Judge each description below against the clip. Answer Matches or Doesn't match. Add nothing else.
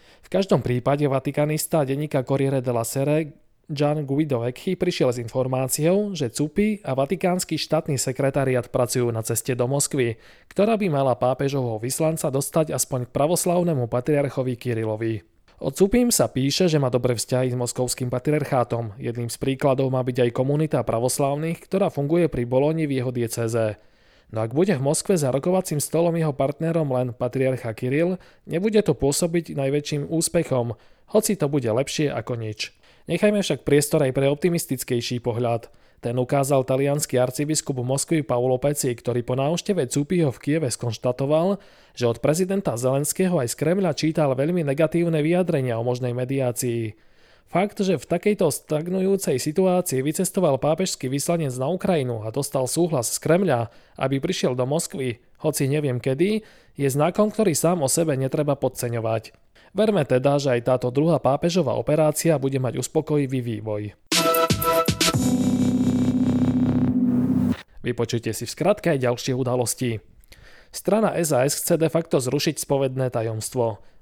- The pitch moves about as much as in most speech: Matches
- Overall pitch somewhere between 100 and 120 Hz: Doesn't match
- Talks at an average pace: Matches